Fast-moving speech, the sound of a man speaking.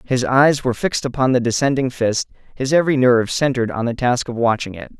Yes: fast, 215 wpm; male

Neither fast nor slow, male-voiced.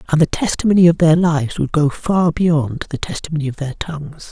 No: fast, 210 wpm; male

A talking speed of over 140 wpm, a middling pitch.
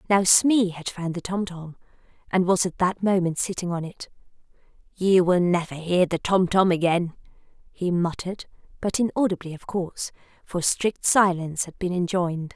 Yes: average, 165 wpm; medium, 180 Hz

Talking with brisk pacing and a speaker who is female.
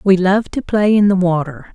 Yes: fast, 240 wpm; female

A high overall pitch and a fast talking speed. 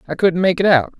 No: medium, 170 Hz; fast, 300 wpm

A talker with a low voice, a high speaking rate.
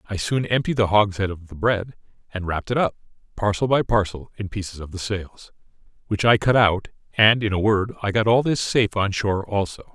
Yes: low, 105 Hz; fast, 215 wpm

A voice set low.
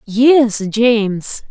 No: high, 225 Hz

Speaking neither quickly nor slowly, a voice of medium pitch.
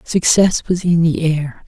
Yes: average, 180 wpm; medium, 165 Hz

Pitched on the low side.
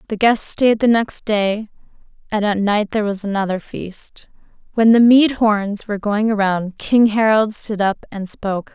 No: high, 210 Hz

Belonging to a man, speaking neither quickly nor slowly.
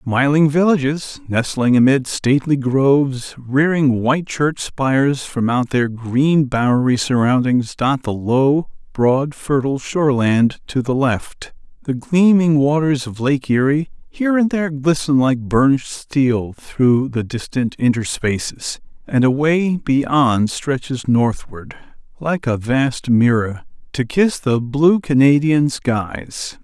No: male; slow, 130 wpm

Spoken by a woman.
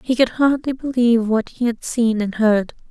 Yes: female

